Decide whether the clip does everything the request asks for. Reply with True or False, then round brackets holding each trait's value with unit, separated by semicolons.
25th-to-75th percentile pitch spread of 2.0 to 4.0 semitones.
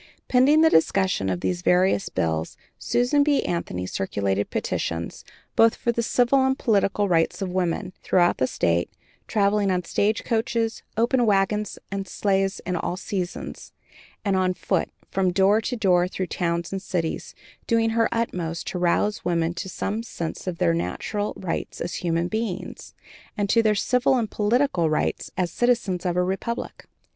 False (4.4 semitones)